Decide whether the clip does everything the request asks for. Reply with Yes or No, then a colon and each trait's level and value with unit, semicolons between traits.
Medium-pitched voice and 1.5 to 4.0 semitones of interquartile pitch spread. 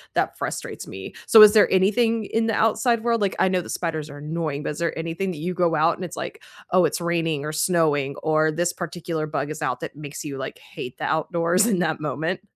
Yes: medium, 165 Hz; average, 3.3 semitones